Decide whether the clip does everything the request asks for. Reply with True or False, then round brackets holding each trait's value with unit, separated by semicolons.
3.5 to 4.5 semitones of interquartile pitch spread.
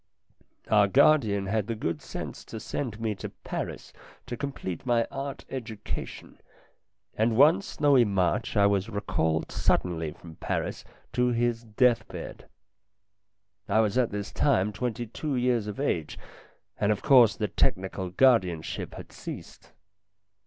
True (4.0 semitones)